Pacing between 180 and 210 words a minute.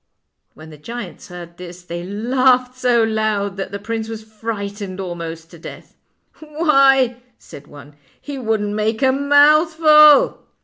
No: average, 160 wpm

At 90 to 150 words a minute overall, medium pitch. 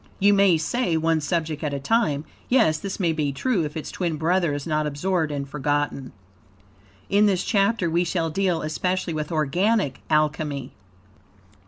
No: average, 165 wpm; medium, 160 Hz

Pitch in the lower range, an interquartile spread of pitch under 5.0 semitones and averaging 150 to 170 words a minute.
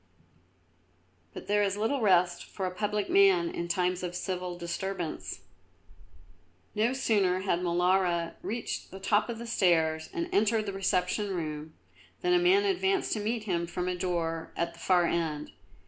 No: medium, 185 Hz; average, 4.0 semitones; average, 165 wpm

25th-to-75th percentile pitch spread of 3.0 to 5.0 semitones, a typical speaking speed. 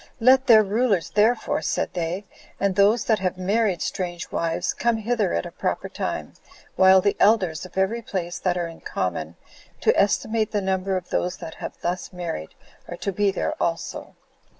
Yes: average, 3.4 semitones; average, 180 wpm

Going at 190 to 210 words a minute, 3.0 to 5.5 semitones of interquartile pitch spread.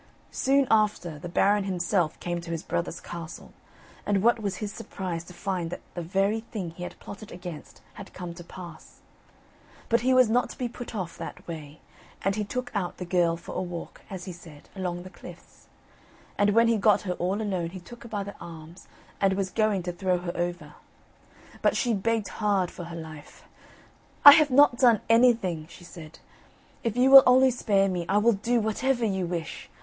Yes: average, 200 wpm; average, 4.2 semitones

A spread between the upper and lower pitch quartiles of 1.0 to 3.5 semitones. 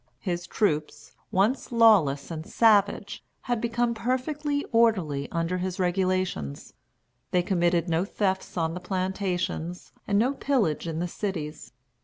No: average, 4.8 semitones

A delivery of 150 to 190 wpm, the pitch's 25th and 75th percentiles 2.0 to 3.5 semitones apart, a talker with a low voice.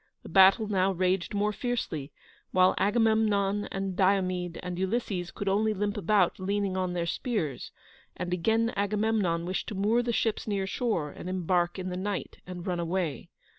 No: average, 170 wpm; narrow, 2.6 semitones; high, 195 Hz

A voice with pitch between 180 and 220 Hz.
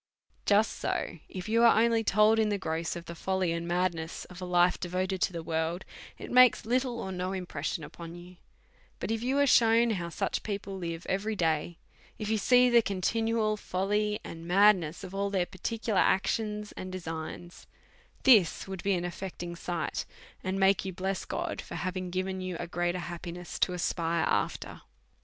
Yes: medium, 185 Hz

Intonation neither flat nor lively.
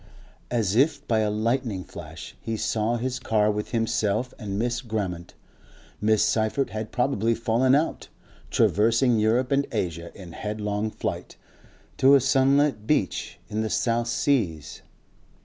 Yes: average, 3.0 semitones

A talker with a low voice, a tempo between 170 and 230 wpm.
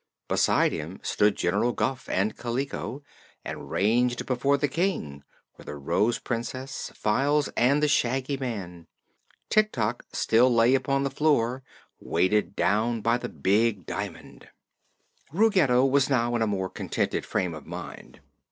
No: low, 120 Hz; average, 145 wpm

